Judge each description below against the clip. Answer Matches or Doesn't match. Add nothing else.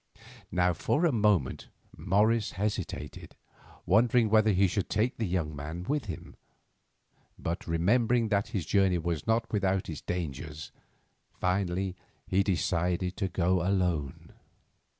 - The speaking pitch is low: Matches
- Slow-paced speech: Matches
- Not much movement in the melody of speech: Doesn't match